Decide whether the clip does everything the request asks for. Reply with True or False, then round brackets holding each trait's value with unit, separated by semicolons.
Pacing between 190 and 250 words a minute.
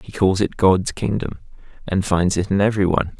True (205 wpm)